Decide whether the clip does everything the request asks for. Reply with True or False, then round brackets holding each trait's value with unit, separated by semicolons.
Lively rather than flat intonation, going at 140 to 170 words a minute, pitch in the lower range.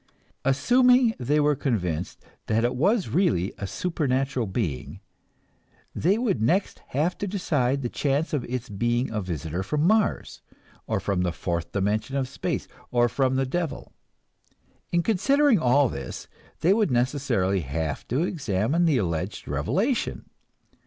True (9.0 semitones; 145 wpm; 130 Hz)